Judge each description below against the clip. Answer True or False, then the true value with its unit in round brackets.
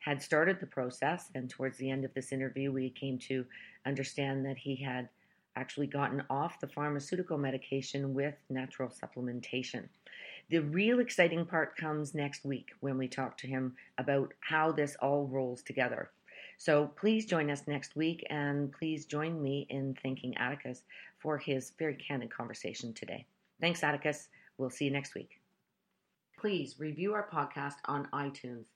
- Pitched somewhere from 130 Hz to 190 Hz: True (140 Hz)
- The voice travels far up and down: False (2.5 semitones)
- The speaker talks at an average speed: True (160 wpm)